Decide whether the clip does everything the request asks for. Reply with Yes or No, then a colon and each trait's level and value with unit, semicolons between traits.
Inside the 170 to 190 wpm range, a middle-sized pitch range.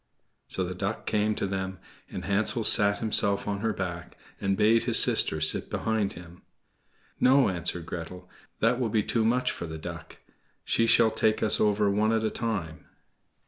Yes: average, 180 wpm; average, 3.4 semitones